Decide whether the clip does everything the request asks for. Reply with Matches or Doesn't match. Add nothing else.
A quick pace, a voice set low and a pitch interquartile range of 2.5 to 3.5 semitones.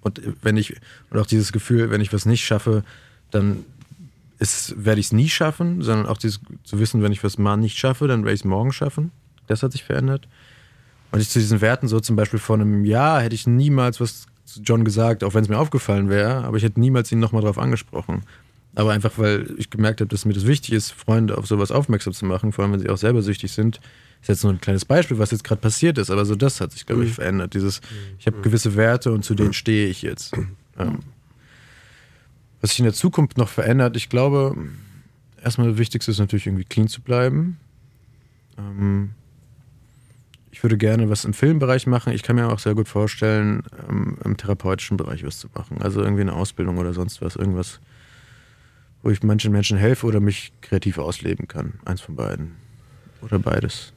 Matches